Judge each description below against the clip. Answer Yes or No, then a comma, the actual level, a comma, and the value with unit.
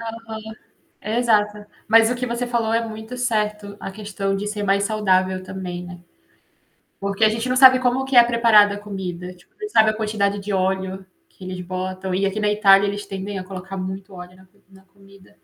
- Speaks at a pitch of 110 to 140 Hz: No, high, 205 Hz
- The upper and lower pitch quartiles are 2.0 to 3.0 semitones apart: Yes, narrow, 2.6 semitones